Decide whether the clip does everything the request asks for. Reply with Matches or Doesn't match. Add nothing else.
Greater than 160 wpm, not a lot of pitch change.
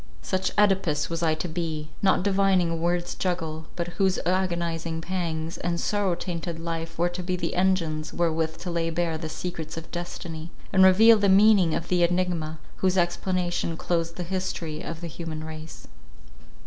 Matches